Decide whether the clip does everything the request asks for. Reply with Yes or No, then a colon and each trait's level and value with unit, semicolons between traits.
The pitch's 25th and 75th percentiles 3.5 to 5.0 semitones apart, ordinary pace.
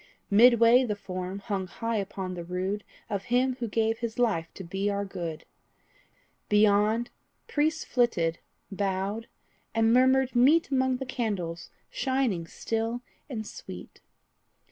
No: average, 4.2 semitones; slow, 130 wpm